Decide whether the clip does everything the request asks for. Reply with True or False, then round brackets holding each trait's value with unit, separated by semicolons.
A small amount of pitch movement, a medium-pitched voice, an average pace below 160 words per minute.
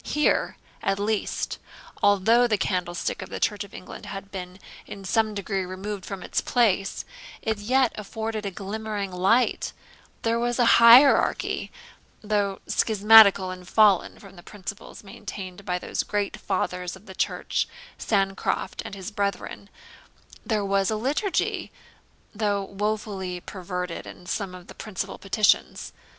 False (2.3 semitones; 200 Hz; 140 wpm)